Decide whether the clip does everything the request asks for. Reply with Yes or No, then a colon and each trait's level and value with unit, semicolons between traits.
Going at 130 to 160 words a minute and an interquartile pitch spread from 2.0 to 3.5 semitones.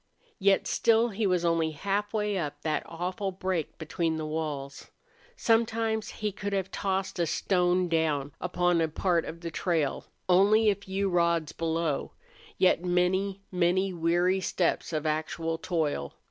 Yes: average, 145 wpm; average, 3.2 semitones